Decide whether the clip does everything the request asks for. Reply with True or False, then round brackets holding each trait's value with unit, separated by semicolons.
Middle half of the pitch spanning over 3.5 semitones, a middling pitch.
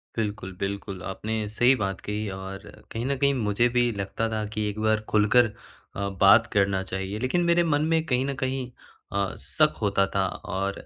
False (4.1 semitones; 105 Hz)